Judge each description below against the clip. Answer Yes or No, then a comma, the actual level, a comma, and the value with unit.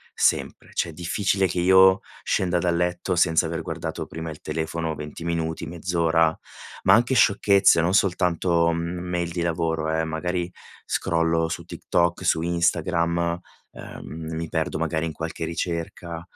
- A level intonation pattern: Yes, narrow, 1.4 semitones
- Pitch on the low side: Yes, very low, 85 Hz